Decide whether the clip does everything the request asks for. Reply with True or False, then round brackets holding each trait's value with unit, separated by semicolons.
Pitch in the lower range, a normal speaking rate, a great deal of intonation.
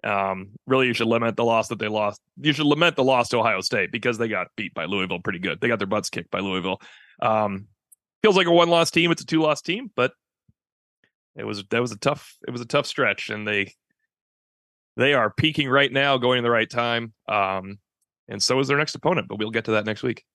False (120 Hz; 245 wpm; 5.8 semitones)